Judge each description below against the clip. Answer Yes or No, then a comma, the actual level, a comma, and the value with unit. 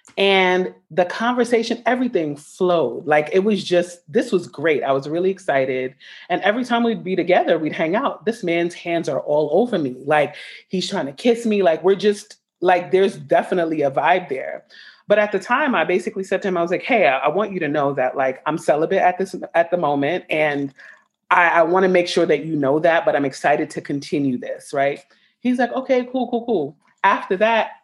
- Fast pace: Yes, fast, 220 wpm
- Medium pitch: Yes, medium, 180 Hz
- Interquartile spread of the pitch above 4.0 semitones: Yes, average, 5.2 semitones